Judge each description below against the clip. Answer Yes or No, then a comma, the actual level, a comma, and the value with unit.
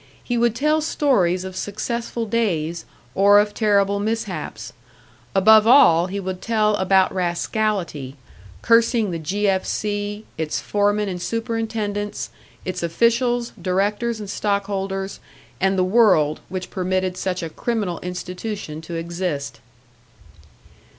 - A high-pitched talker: Yes, high, 200 Hz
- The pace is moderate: No, slow, 125 wpm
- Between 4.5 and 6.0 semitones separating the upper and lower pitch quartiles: No, average, 3.2 semitones